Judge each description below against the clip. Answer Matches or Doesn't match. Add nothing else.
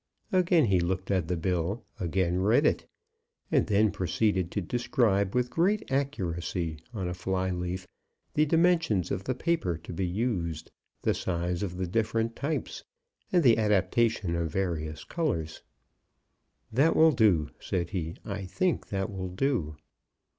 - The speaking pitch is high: Doesn't match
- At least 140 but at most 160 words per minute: Matches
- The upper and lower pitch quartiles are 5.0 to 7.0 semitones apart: Matches